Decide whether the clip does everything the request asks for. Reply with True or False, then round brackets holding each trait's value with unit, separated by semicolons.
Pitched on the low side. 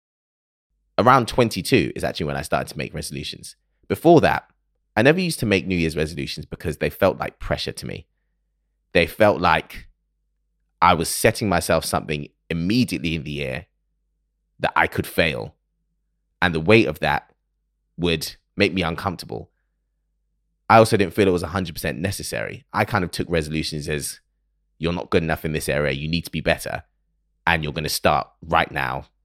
True (80 Hz)